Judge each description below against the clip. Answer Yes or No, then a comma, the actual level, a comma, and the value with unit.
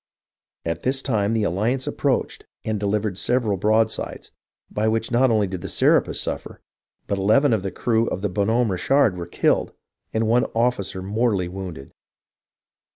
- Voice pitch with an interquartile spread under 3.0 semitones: No, average, 3.3 semitones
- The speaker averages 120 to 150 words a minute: No, average, 160 wpm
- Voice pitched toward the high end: No, low, 105 Hz